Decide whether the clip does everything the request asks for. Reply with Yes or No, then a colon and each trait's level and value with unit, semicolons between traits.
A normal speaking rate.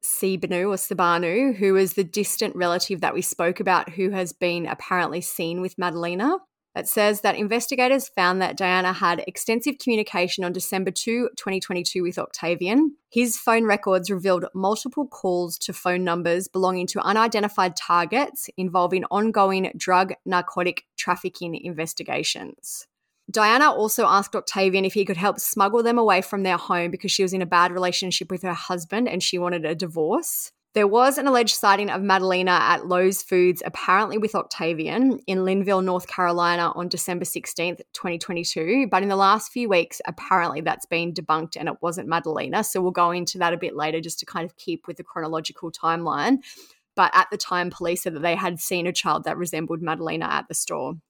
Yes: average, 180 wpm